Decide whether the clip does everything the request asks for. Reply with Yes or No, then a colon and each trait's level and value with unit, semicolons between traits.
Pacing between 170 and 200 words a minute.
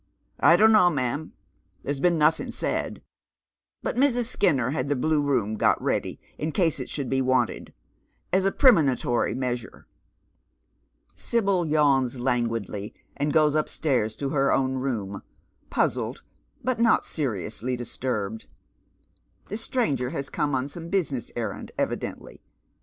No: average, 140 wpm